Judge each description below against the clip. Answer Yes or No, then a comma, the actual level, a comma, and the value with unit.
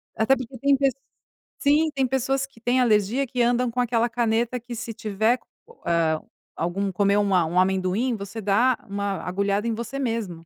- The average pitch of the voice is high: Yes, high, 230 Hz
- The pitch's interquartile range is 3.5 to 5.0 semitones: Yes, average, 3.9 semitones